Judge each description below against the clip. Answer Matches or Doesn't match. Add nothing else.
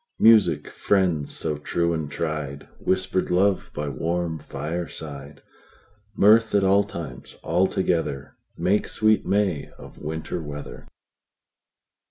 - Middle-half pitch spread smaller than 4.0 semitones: Doesn't match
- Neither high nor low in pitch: Doesn't match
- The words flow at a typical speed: Doesn't match